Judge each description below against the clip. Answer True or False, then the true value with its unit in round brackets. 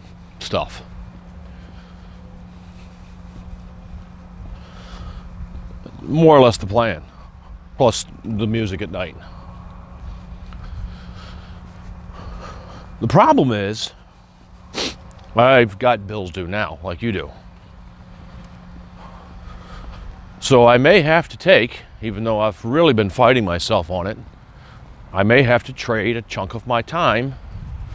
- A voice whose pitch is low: True (90 Hz)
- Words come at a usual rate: False (100 wpm)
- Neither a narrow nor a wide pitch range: True (4.1 semitones)